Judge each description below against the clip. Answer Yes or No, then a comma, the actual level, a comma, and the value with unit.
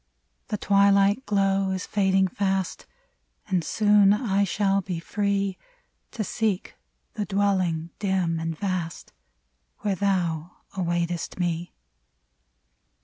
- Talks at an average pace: No, slow, 105 wpm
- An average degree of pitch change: No, narrow, 2.3 semitones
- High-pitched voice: Yes, high, 195 Hz